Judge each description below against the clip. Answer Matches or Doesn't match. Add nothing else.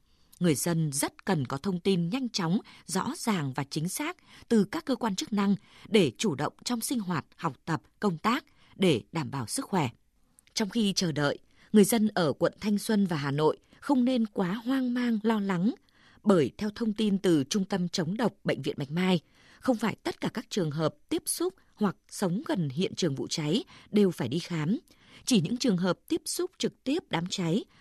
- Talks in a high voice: Matches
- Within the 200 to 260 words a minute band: Matches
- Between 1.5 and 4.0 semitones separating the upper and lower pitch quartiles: Doesn't match